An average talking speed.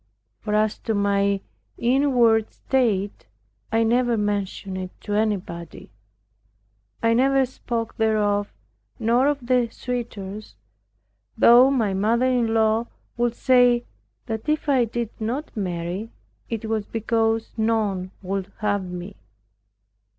No: slow, 120 wpm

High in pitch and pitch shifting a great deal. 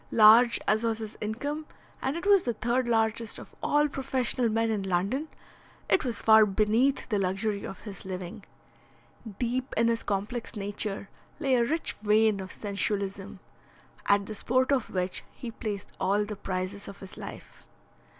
No: high, 220 Hz; average, 3.5 semitones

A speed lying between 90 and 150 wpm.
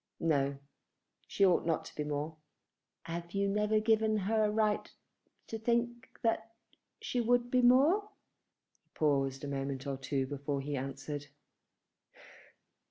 Yes: average, 140 wpm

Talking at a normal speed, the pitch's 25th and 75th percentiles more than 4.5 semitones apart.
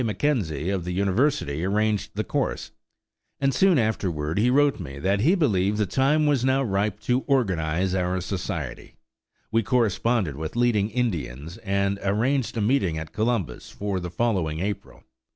Yes: average, 155 wpm; average, 5.3 semitones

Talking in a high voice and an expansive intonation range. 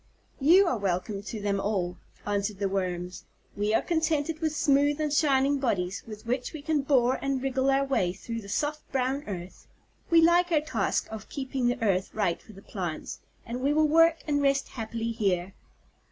Yes: very high, 255 Hz; wide, 6.4 semitones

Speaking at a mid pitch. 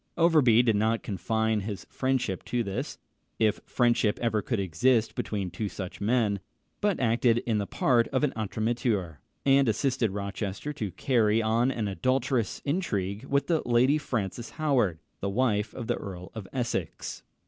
No: low, 115 Hz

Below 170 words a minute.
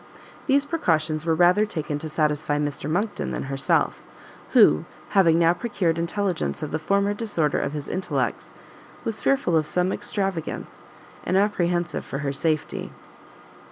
Yes: average, 145 wpm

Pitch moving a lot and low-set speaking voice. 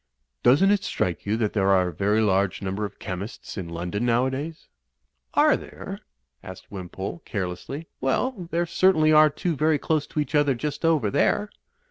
Yes: wide, 8.0 semitones; low, 125 Hz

